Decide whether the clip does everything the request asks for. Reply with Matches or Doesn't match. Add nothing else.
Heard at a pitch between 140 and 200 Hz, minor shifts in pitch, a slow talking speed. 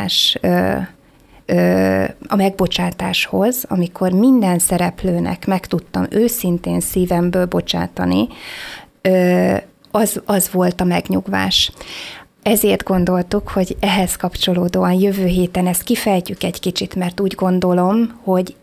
Matches